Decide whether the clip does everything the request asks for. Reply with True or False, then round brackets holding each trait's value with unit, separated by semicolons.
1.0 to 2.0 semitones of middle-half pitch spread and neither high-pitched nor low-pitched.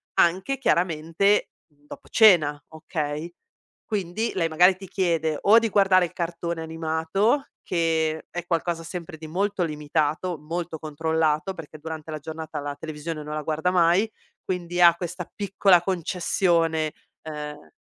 False (2.5 semitones; 165 Hz)